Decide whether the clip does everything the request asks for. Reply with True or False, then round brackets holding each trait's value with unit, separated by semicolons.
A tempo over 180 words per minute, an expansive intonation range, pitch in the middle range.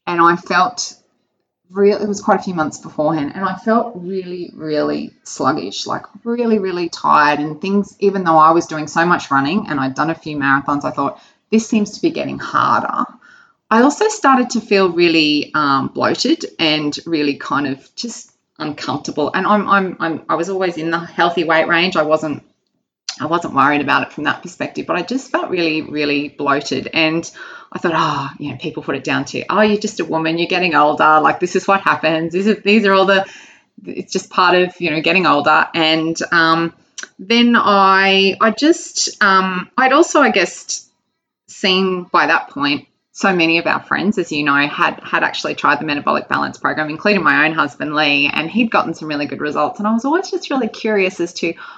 False (205 wpm; 4.9 semitones; 180 Hz)